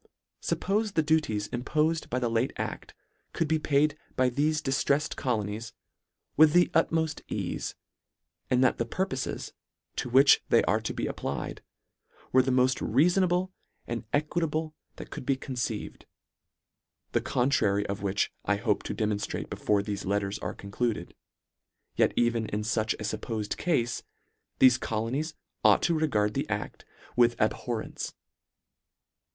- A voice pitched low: Yes, low, 125 Hz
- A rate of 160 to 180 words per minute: No, average, 145 wpm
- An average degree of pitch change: No, wide, 5.9 semitones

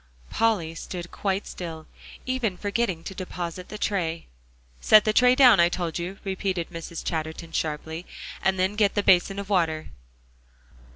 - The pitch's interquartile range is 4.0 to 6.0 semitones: No, average, 3.4 semitones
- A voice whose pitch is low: No, medium, 185 Hz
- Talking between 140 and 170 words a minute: Yes, average, 155 wpm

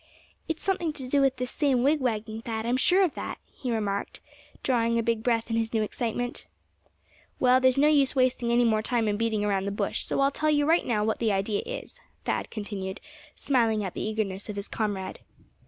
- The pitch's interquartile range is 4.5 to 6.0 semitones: No, average, 3.5 semitones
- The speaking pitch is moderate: No, high, 230 Hz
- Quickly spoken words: Yes, fast, 210 wpm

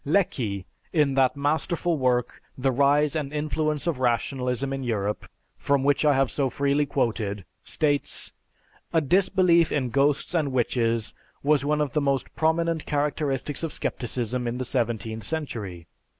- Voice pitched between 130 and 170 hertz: Yes, medium, 140 Hz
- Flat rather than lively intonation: No, average, 3.6 semitones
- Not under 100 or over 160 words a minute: Yes, average, 150 wpm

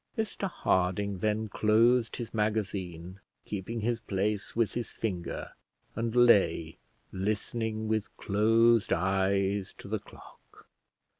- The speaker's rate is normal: No, slow, 115 wpm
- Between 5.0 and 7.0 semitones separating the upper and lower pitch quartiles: No, average, 2.8 semitones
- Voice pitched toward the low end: Yes, low, 105 Hz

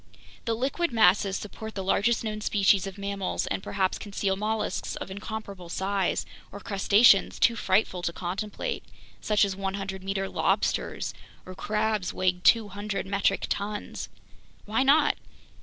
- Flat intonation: Yes, narrow, 2.0 semitones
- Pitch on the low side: No, high, 200 Hz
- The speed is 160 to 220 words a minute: No, average, 140 wpm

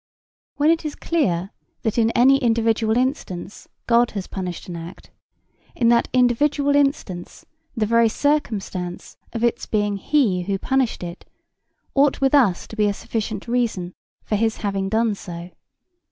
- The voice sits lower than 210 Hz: No, high, 225 Hz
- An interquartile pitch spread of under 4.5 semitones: No, average, 4.8 semitones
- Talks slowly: No, average, 155 wpm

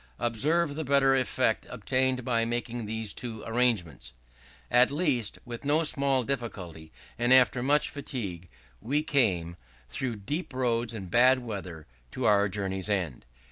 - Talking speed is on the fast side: No, average, 140 wpm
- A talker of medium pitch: No, low, 120 Hz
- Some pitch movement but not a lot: Yes, average, 4.5 semitones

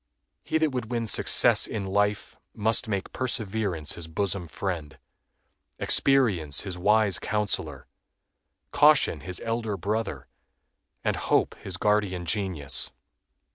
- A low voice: Yes, low, 100 Hz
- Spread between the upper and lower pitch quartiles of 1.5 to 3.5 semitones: No, average, 4.1 semitones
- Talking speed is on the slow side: Yes, slow, 115 wpm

